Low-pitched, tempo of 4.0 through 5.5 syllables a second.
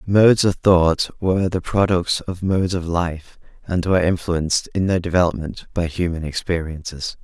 Yes: very low, 90 Hz; 5.0 syllables/s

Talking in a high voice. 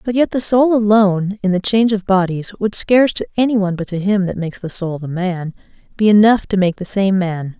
Yes: high, 195 Hz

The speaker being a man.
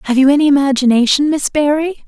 No: female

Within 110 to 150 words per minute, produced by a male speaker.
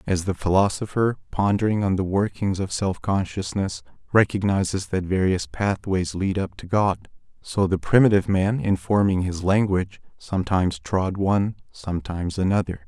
Yes: average, 145 wpm; male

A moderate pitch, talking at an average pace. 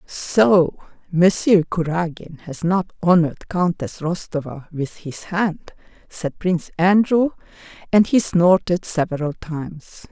No: medium, 170 Hz; slow, 115 wpm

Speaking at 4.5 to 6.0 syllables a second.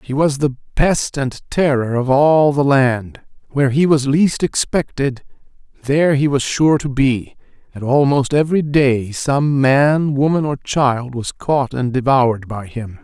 No: 4.1 syllables/s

